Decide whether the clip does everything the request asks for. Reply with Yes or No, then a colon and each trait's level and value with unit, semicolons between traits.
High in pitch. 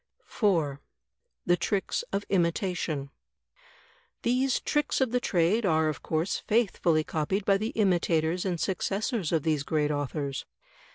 No: medium, 175 Hz